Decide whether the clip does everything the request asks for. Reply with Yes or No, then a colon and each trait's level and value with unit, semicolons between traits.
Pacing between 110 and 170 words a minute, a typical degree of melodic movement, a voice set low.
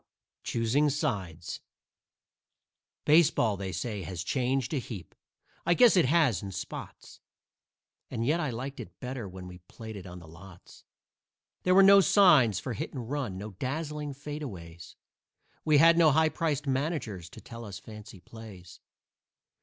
No: average, 155 wpm; wide, 7.6 semitones; low, 125 Hz